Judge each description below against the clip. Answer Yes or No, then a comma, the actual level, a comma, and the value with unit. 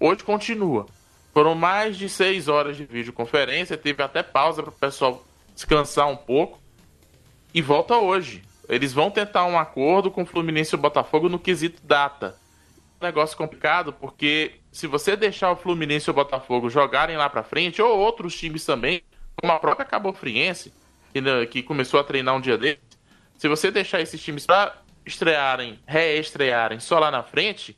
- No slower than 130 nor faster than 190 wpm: Yes, average, 165 wpm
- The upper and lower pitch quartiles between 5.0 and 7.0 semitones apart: No, average, 4.2 semitones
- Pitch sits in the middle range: Yes, medium, 155 Hz